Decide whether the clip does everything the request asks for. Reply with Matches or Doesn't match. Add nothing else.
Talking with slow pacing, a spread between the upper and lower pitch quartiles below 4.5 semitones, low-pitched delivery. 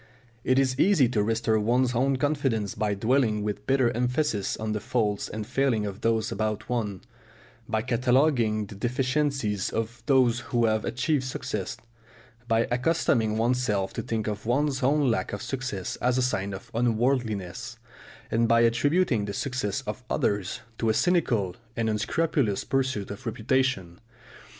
Doesn't match